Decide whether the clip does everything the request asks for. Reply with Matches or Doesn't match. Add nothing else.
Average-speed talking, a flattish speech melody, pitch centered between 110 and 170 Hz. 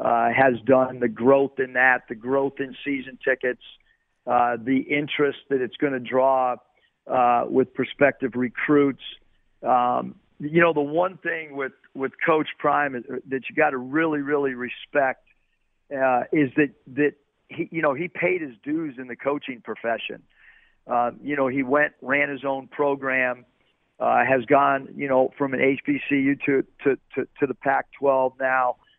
Matches